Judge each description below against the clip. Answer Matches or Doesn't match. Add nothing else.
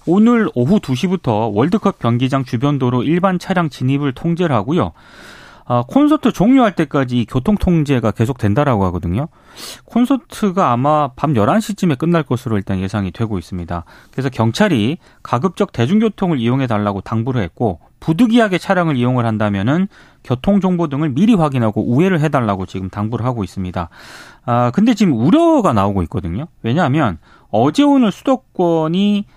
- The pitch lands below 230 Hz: Matches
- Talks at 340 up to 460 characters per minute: Matches